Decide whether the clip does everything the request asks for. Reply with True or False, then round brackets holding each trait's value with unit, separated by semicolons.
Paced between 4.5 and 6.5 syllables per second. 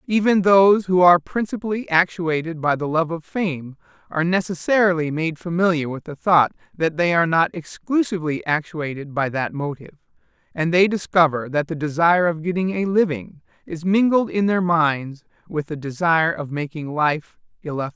True (5.3 syllables/s)